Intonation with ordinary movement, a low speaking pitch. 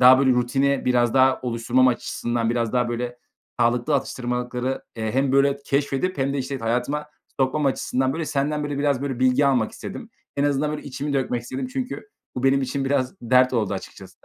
No: narrow, 2.3 semitones; low, 130 Hz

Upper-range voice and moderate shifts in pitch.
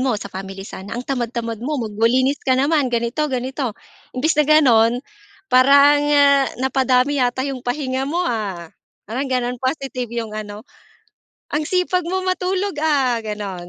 Yes: very high, 255 Hz; average, 3.8 semitones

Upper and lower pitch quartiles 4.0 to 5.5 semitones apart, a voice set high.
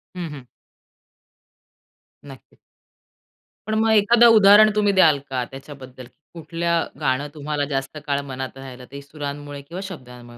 No: average, 4.3 semitones; medium, 145 Hz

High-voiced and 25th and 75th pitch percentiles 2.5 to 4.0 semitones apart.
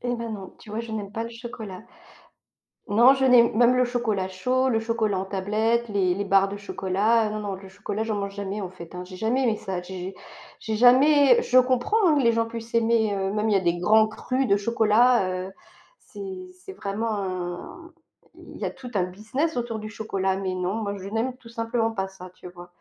Yes: high, 215 Hz; average, 3.6 semitones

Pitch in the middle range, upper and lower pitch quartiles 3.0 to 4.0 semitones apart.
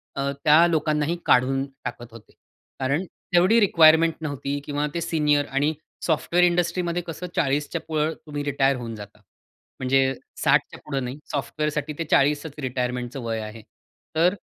Yes: medium, 145 Hz; average, 3.3 semitones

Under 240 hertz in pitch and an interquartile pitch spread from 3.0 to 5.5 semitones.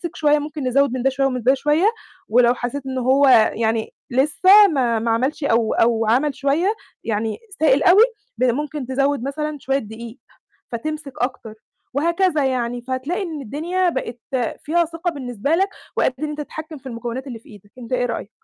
No: very high, 270 Hz; average, 4.0 semitones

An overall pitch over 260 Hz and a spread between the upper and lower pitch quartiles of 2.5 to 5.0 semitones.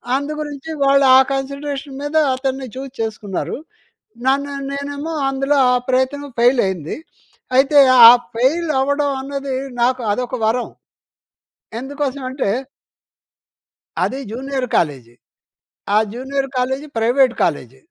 No: very high, 270 Hz; narrow, 2.1 semitones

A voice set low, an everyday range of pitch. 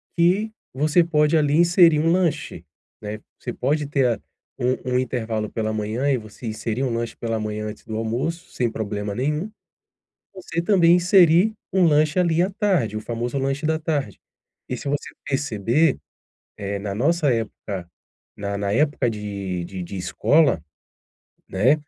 No: low, 130 Hz; wide, 7.0 semitones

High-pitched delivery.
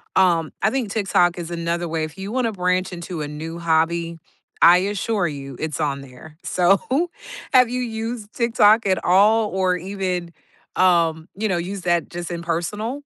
No: medium, 180 Hz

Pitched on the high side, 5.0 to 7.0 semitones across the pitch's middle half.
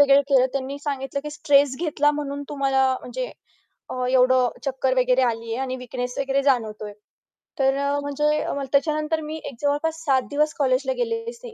No: very high, 280 Hz; narrow, 2.5 semitones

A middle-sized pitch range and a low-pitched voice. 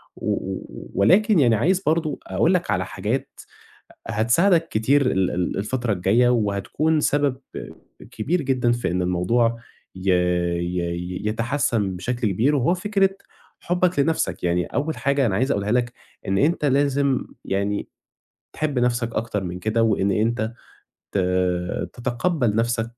No: wide, 6.3 semitones; low, 120 Hz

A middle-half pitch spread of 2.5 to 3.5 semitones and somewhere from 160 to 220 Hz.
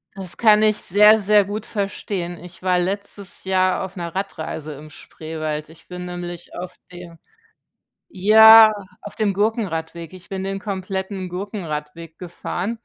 Yes: average, 2.9 semitones; medium, 185 Hz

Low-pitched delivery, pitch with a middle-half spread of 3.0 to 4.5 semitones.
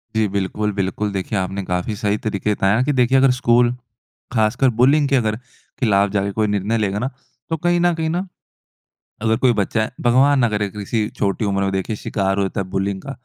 Yes: low, 105 Hz; average, 4.0 semitones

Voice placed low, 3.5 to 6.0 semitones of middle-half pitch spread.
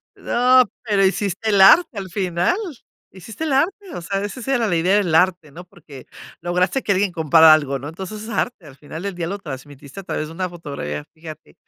No: medium, 180 Hz; average, 4.4 semitones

